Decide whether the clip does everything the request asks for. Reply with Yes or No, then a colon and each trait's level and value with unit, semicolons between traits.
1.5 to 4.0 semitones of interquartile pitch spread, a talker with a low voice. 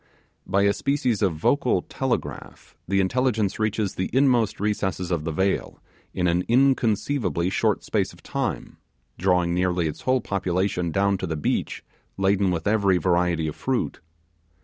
Yes: average, 3.4 semitones; very low, 95 Hz